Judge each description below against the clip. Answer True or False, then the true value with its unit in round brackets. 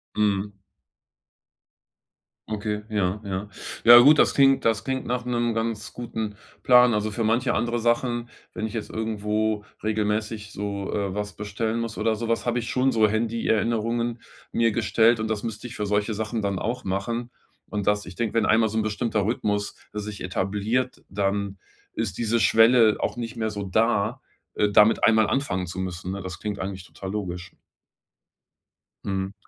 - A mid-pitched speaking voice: False (110 Hz)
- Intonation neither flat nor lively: False (2.3 semitones)